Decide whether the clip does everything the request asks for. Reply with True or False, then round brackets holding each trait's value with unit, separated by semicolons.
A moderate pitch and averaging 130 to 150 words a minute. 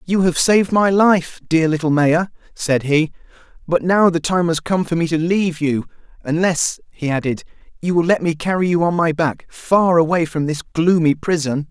False (165 Hz; 195 wpm)